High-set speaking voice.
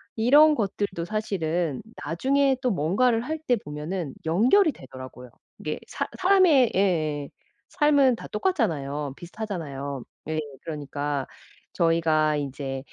No: medium, 170 Hz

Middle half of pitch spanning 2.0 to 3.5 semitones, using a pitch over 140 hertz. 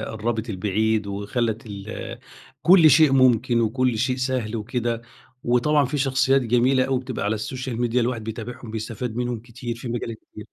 No: narrow, 2.6 semitones; low, 120 Hz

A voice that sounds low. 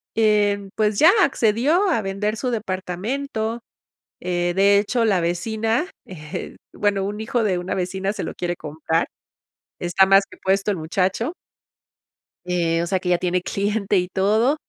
No: high, 195 Hz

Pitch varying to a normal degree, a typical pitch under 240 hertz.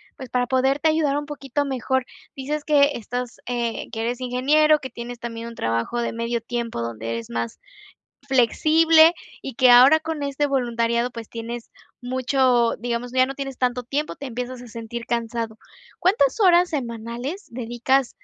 No: average, 3.0 semitones; very high, 250 Hz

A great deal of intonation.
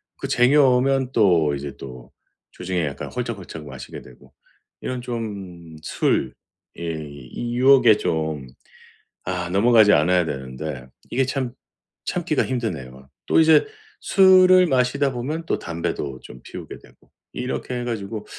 Yes: wide, 8.5 semitones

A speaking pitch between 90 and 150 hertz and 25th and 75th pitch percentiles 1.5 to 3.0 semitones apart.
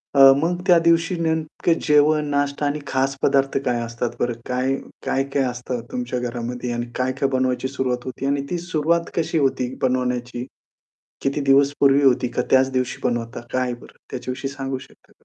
Yes: low, 135 Hz; narrow, 2.4 semitones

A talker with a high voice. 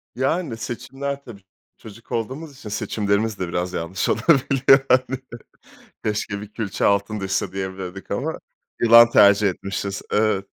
No: low, 110 Hz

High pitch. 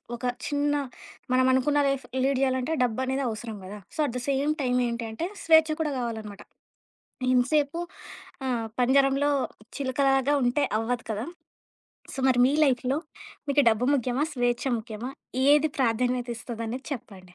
Yes: very high, 255 Hz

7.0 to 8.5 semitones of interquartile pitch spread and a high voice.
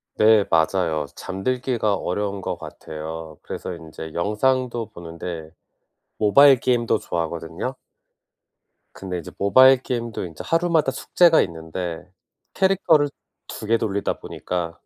No: wide, 7.3 semitones; low, 100 Hz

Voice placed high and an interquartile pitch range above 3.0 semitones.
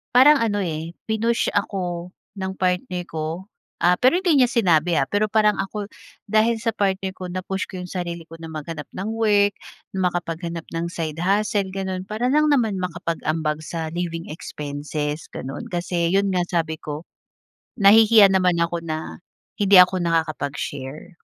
No: medium, 180 Hz; average, 3.7 semitones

